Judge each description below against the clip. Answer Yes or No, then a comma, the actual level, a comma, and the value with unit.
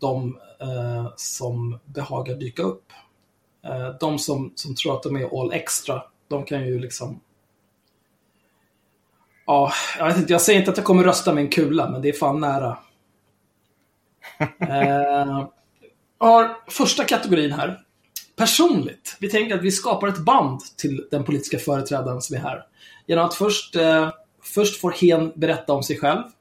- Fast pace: No, average, 160 wpm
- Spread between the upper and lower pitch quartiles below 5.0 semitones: No, average, 5.3 semitones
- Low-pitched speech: No, medium, 145 Hz